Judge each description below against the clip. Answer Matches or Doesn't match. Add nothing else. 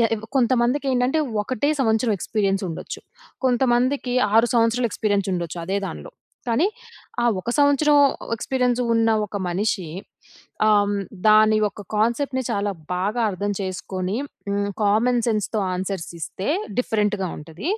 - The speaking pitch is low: Doesn't match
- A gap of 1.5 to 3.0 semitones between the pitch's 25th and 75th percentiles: Doesn't match